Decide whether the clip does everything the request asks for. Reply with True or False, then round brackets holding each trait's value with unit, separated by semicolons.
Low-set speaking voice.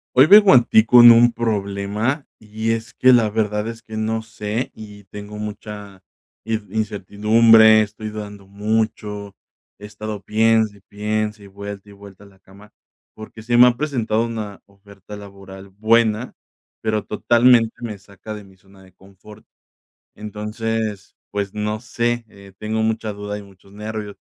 True (105 Hz)